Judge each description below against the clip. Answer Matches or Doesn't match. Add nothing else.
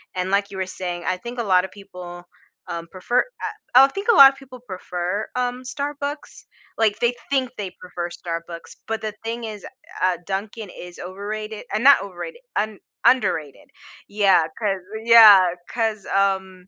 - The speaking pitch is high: Matches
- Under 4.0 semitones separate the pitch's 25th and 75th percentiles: Doesn't match